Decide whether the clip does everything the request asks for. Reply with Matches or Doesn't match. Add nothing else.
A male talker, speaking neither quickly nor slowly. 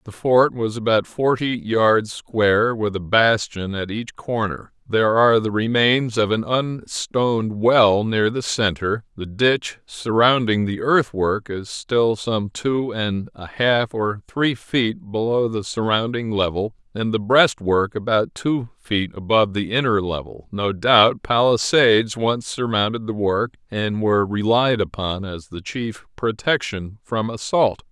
Matches